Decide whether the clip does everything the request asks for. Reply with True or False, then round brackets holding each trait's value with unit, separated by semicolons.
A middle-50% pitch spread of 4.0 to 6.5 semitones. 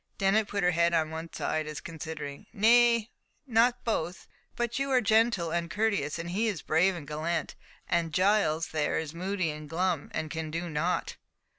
True (5.0 semitones)